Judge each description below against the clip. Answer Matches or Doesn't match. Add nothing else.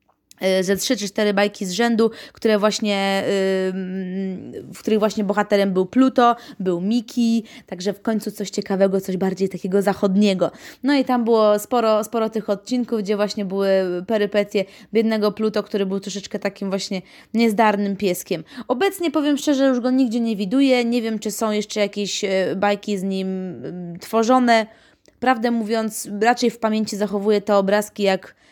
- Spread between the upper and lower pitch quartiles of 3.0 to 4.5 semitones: Doesn't match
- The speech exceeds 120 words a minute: Matches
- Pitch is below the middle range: Doesn't match